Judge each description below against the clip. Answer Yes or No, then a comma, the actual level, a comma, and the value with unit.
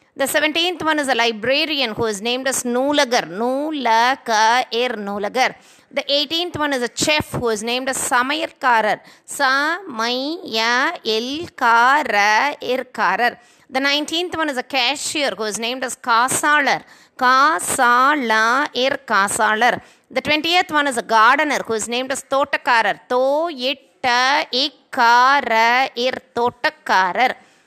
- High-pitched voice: Yes, very high, 255 Hz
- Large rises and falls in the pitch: No, average, 3.5 semitones